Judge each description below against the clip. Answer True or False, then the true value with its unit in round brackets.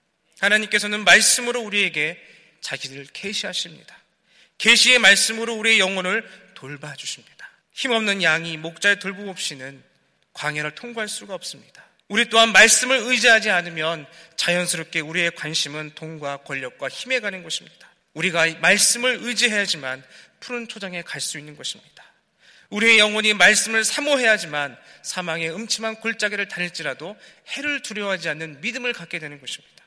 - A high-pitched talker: True (195 Hz)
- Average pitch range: False (5.7 semitones)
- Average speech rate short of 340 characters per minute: False (360 characters per minute)